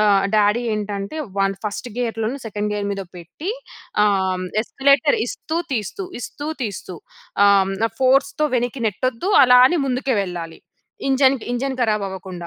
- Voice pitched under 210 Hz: No, high, 220 Hz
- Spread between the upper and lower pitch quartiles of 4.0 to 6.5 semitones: Yes, average, 4.7 semitones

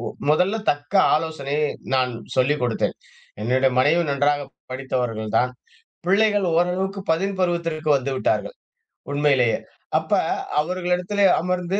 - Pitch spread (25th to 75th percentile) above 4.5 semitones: Yes, wide, 5.4 semitones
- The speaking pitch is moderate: Yes, medium, 155 Hz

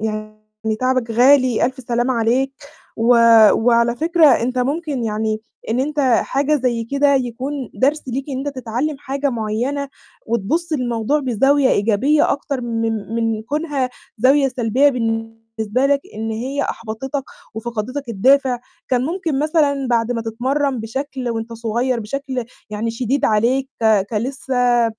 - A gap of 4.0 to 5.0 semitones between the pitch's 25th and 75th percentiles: No, average, 3.5 semitones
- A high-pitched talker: Yes, very high, 250 Hz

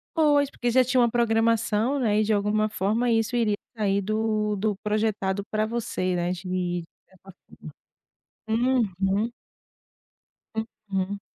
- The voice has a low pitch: No, high, 215 Hz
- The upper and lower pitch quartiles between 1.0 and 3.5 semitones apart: Yes, average, 2.8 semitones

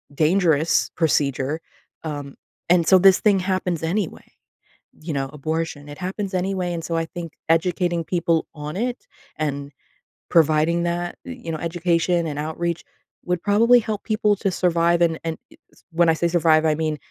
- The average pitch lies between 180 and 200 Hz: No, medium, 170 Hz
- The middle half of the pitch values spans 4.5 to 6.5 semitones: No, narrow, 2.4 semitones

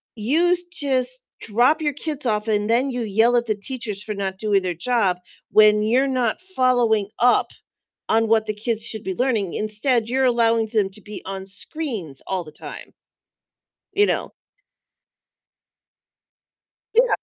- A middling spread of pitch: Yes, average, 3.5 semitones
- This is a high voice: Yes, high, 225 Hz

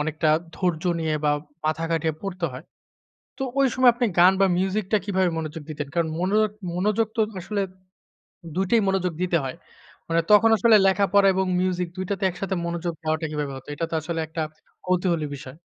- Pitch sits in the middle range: Yes, medium, 180 Hz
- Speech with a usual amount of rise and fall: Yes, average, 3.4 semitones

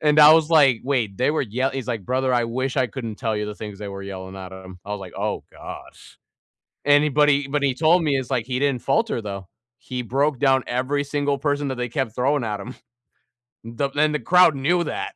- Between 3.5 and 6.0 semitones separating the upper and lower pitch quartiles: Yes, average, 4.4 semitones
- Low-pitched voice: Yes, low, 130 Hz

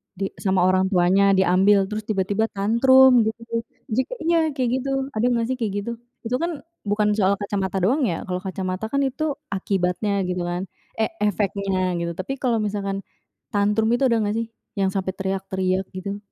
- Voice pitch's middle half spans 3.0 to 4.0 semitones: Yes, average, 3.6 semitones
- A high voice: Yes, high, 205 Hz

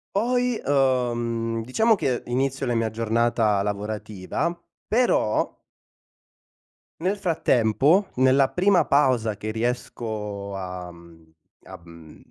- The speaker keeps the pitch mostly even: No, average, 4.7 semitones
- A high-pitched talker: No, low, 115 Hz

